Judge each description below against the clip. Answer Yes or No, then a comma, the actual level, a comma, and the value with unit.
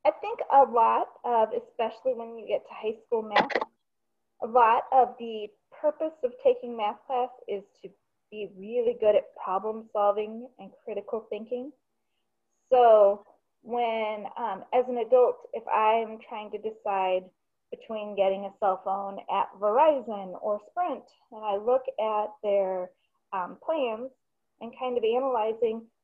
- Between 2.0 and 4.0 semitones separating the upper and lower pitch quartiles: Yes, average, 3.4 semitones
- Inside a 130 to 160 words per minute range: Yes, average, 145 wpm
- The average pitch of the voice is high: Yes, high, 225 Hz